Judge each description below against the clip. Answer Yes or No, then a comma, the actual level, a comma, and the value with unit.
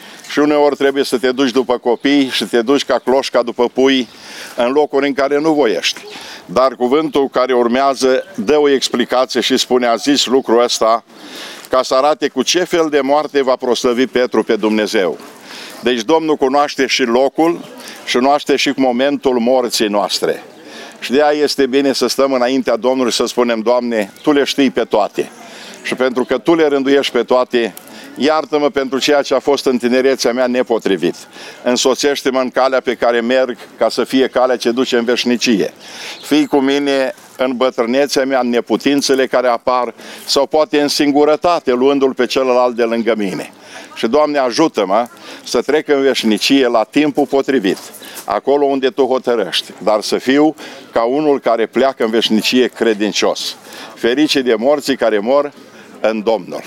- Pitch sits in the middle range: No, low, 130 Hz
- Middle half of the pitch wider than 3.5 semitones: No, narrow, 2.4 semitones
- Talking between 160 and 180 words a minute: Yes, fast, 170 wpm